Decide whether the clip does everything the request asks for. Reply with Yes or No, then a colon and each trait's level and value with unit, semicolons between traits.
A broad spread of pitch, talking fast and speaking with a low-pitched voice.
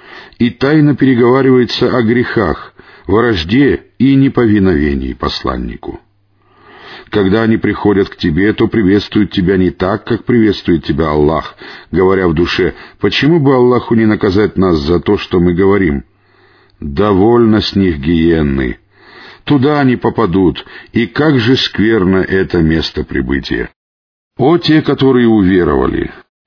No: wide, 6.0 semitones; average, 125 wpm; low, 105 Hz